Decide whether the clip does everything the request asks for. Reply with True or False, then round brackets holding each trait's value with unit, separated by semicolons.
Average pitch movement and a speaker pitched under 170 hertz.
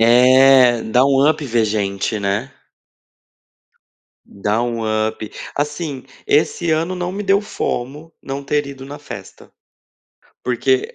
True (4.2 semitones; 135 Hz)